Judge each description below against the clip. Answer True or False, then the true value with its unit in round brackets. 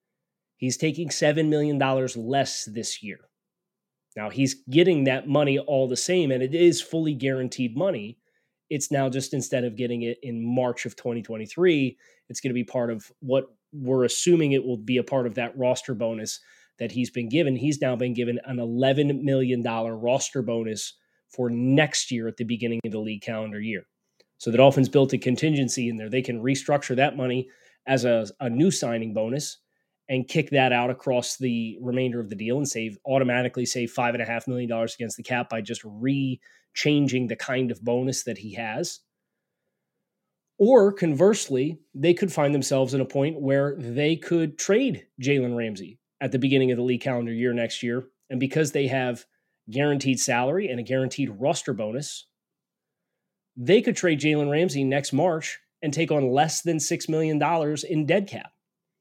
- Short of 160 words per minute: False (180 wpm)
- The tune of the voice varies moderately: True (3.2 semitones)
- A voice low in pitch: True (130 Hz)